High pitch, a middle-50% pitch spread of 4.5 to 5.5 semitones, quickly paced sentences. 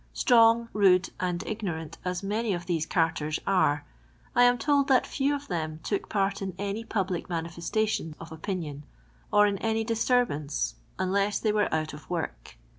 No: high, 195 Hz; average, 5.2 semitones; average, 165 wpm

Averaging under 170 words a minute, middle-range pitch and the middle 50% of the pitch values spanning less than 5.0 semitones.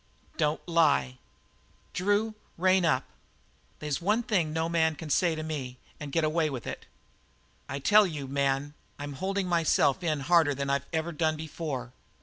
Yes: average, 160 wpm; medium, 155 Hz; average, 3.5 semitones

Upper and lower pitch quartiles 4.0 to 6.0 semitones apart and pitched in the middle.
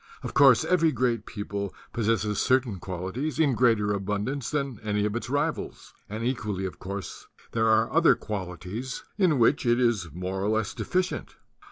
No: average, 4.4 semitones; low, 115 Hz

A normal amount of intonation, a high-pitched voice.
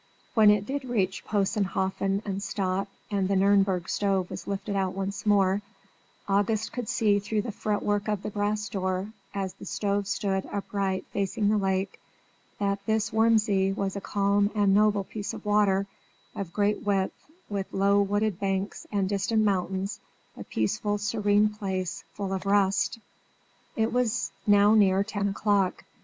No: narrow, 1.3 semitones; high, 200 Hz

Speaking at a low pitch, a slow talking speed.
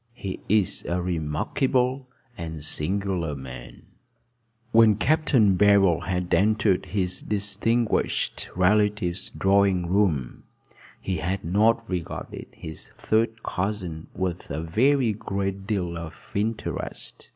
Yes: very low, 95 Hz; slow, 105 wpm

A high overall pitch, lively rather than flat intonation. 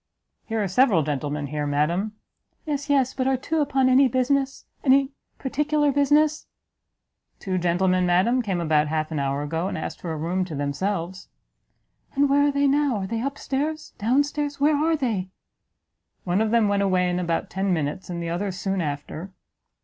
Yes: high, 200 Hz; wide, 8.3 semitones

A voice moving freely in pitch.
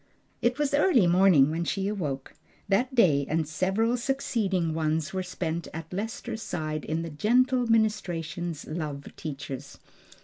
Yes: wide, 6.0 semitones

